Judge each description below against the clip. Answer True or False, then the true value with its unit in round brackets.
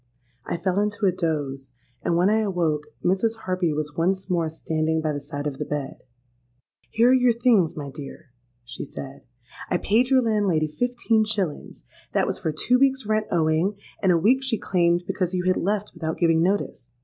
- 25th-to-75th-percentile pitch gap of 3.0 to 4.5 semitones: False (5.3 semitones)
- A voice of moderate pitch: True (180 Hz)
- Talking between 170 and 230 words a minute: True (190 wpm)